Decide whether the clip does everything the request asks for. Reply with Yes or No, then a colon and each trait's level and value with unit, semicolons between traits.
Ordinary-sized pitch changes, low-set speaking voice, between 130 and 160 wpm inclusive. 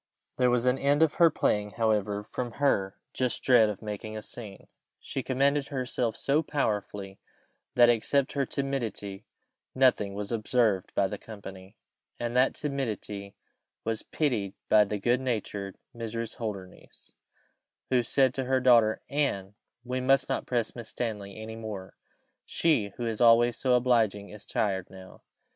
Yes: average, 3.8 semitones; low, 115 Hz; average, 155 wpm